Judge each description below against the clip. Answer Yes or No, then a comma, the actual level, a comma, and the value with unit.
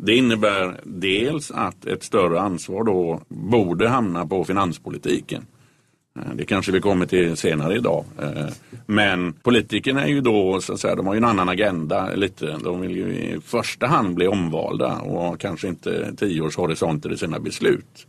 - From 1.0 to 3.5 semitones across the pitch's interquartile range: Yes, average, 3.1 semitones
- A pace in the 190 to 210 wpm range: No, average, 160 wpm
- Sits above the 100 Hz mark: No, very low, 95 Hz